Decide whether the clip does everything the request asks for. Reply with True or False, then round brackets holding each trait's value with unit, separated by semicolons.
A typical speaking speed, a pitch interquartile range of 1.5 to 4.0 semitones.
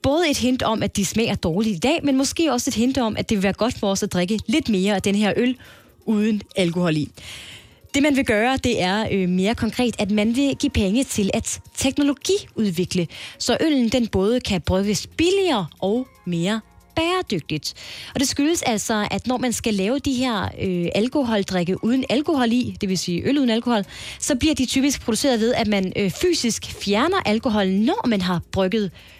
False (205 wpm; 5.1 semitones)